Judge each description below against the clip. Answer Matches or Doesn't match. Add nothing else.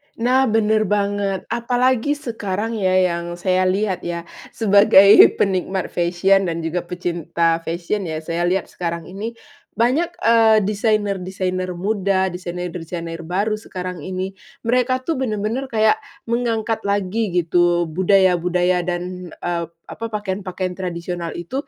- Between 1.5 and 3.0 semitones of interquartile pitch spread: Doesn't match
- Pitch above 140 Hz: Matches